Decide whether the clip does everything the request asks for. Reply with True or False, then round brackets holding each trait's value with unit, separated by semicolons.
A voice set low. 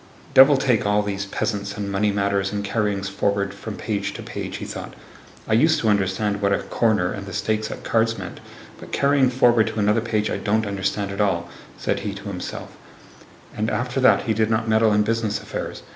True (105 Hz)